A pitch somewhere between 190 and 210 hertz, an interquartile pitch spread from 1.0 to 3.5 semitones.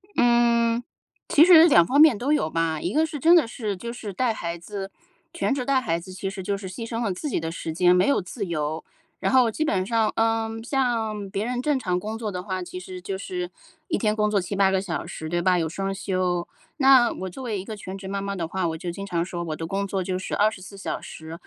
No: high, 200 Hz; average, 4.6 semitones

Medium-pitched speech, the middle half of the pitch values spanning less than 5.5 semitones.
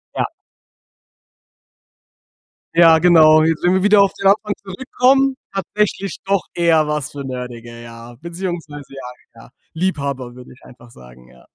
No: medium, 160 Hz; wide, 7.2 semitones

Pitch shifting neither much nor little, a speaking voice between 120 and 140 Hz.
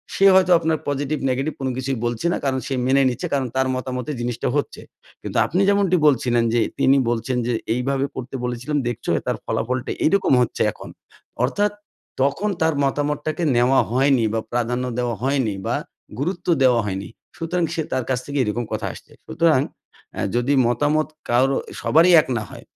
Yes: average, 3.7 semitones; low, 135 Hz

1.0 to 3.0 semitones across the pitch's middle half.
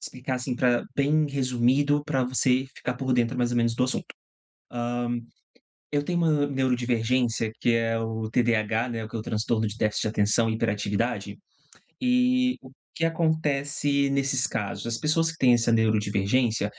No: average, 3.7 semitones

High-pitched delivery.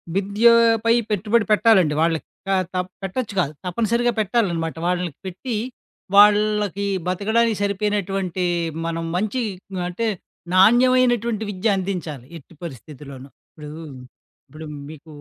Yes: high, 200 Hz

